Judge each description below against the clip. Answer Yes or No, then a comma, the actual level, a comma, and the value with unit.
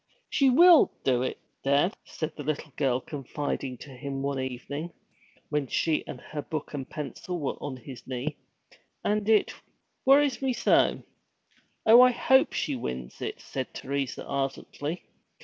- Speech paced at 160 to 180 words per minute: No, average, 150 wpm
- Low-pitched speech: No, medium, 145 Hz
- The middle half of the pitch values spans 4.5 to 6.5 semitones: Yes, average, 5.1 semitones